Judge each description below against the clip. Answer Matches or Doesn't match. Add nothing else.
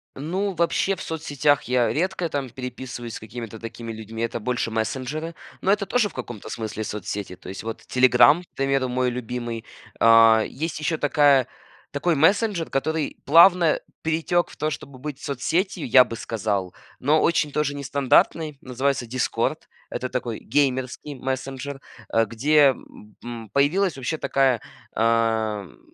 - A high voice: Doesn't match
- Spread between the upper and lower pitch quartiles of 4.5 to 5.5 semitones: Matches